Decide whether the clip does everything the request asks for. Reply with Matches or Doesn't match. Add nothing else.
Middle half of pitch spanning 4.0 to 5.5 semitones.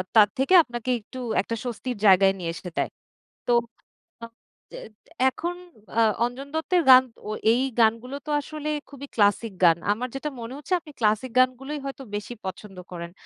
Matches